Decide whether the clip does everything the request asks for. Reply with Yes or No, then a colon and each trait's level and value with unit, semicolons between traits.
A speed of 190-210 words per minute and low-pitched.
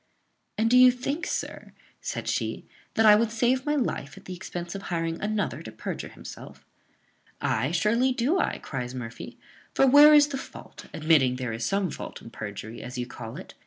No: average, 195 wpm; high, 190 Hz